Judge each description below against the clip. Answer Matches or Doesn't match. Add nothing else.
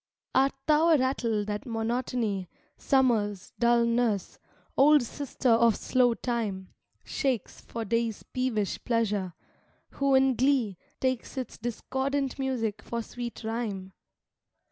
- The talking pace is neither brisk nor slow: Doesn't match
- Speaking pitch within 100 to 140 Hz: Doesn't match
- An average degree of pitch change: Matches